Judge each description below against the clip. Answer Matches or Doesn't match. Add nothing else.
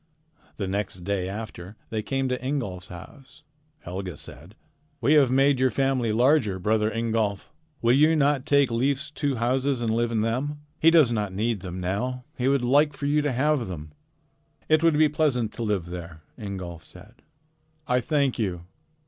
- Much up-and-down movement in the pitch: Matches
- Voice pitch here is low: Matches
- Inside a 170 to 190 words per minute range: Matches